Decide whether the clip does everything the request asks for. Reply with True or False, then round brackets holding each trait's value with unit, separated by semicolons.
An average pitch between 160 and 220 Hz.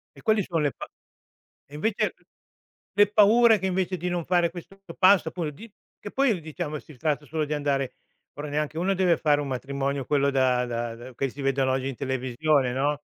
False (150 Hz)